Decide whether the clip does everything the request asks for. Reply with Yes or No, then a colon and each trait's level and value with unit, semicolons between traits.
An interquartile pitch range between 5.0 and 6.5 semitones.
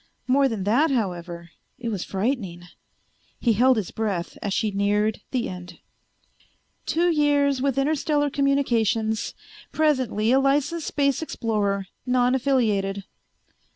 Yes: wide, 5.5 semitones